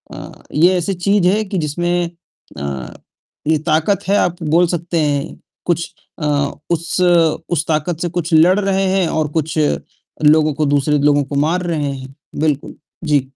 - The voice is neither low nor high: Yes, medium, 160 Hz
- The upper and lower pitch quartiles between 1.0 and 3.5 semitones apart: Yes, average, 2.8 semitones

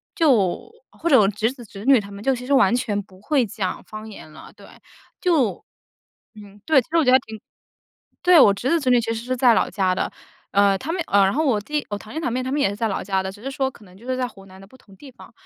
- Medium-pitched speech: No, high, 230 Hz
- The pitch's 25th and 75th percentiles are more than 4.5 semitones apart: Yes, average, 5.0 semitones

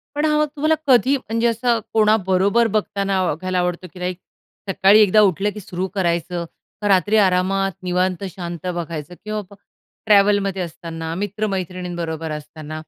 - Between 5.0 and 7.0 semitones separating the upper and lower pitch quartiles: No, average, 3.2 semitones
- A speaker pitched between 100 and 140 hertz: No, high, 190 Hz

